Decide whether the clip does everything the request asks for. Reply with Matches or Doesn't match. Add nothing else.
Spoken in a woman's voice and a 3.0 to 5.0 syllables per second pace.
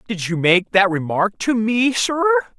Doesn't match